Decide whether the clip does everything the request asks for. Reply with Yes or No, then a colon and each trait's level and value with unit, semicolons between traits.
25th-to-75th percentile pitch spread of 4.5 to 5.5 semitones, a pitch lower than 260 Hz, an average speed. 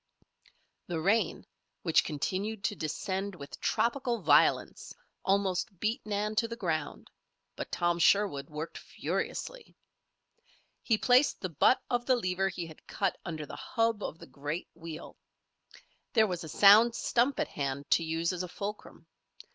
Yes: average, 5.2 semitones; high, 190 Hz; average, 150 wpm